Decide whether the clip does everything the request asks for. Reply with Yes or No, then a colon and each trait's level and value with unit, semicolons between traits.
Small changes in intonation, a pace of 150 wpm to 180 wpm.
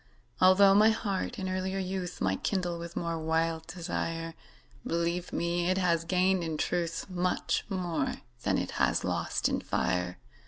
Yes: narrow, 2.1 semitones; average, 155 wpm